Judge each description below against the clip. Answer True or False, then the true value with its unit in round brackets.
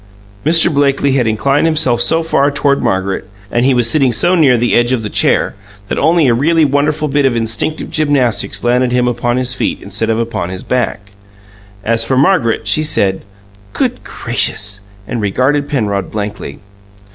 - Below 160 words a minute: False (175 wpm)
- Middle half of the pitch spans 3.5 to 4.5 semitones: True (4.2 semitones)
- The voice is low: True (125 Hz)